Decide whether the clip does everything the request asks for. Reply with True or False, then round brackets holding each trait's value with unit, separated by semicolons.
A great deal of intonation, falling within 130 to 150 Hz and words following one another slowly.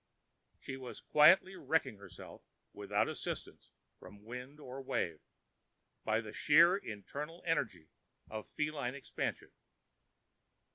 True (5.8 semitones; 135 Hz; 105 wpm)